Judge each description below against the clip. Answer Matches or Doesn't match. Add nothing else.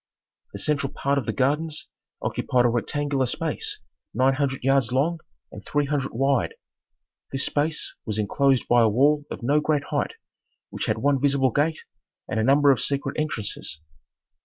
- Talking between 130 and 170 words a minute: Matches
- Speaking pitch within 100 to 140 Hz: Matches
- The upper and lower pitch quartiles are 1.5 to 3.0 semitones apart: Matches